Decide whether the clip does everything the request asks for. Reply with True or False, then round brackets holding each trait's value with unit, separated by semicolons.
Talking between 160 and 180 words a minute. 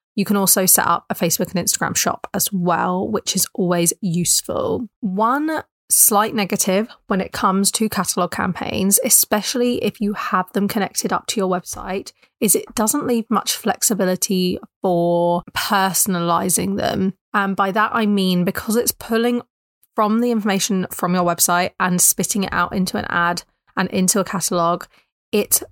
True (165 wpm)